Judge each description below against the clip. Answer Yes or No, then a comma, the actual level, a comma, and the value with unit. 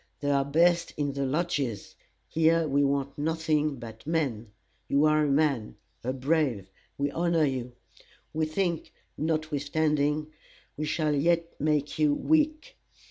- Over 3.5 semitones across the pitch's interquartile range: No, narrow, 2.5 semitones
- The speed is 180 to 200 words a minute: No, slow, 135 wpm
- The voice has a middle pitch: Yes, medium, 150 Hz